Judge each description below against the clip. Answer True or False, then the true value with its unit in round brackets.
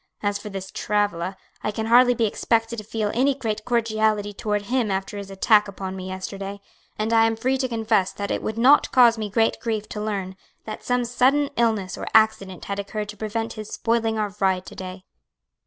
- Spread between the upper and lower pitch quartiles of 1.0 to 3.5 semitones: True (2.4 semitones)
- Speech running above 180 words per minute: True (205 wpm)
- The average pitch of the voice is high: True (215 Hz)